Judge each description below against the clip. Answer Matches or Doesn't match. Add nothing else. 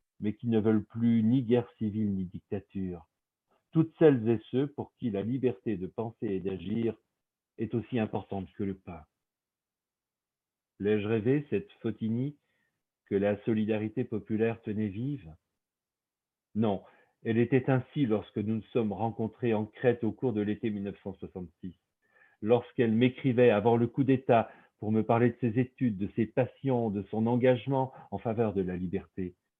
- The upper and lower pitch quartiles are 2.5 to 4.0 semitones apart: Matches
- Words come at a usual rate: Matches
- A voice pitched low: Matches